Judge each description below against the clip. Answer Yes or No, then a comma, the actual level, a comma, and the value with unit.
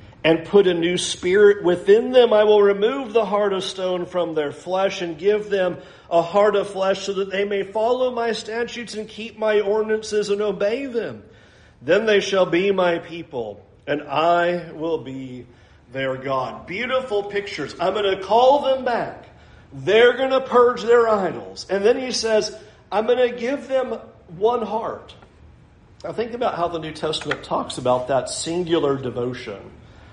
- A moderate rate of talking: Yes, average, 175 wpm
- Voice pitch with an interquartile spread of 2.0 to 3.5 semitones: No, average, 5.2 semitones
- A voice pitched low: No, high, 200 Hz